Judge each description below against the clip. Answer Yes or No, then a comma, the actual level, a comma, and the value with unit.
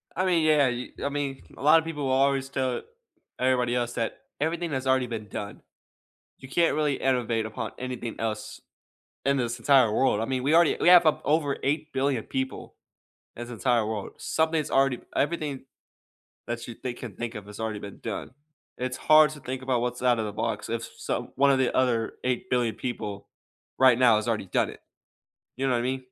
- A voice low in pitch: Yes, low, 130 Hz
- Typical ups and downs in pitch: Yes, average, 3.1 semitones